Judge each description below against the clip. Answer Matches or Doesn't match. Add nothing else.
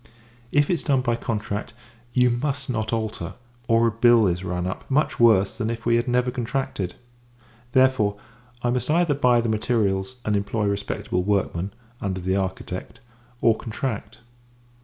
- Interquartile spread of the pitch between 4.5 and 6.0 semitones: Doesn't match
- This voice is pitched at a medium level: Doesn't match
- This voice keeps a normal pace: Matches